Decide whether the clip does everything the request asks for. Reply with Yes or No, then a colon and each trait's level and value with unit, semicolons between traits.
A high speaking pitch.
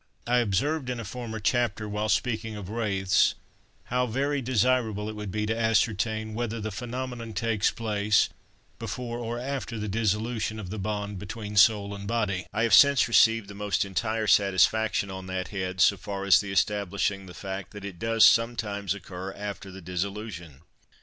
No: low, 105 Hz